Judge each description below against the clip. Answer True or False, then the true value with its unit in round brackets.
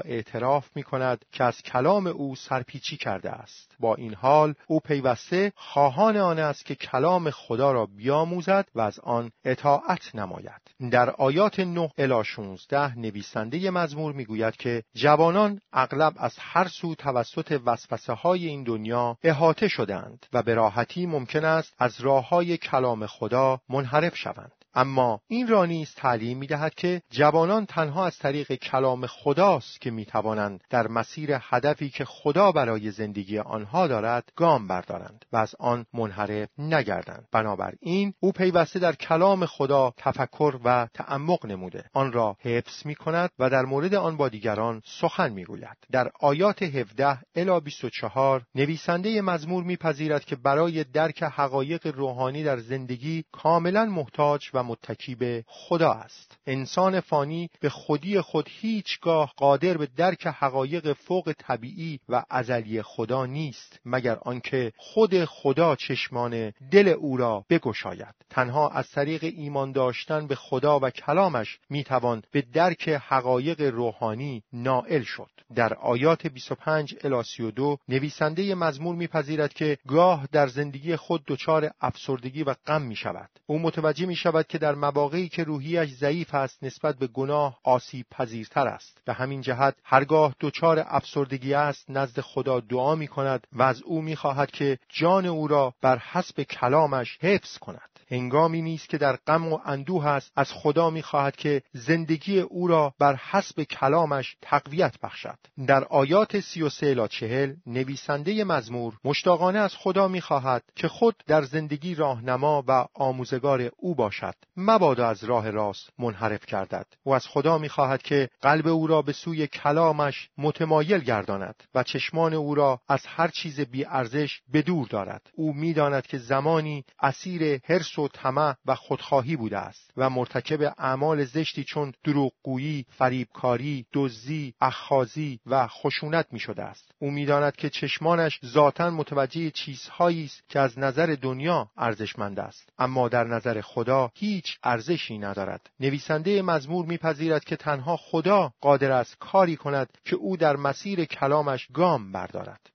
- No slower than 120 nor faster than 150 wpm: True (145 wpm)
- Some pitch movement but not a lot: True (4.1 semitones)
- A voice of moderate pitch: True (145 Hz)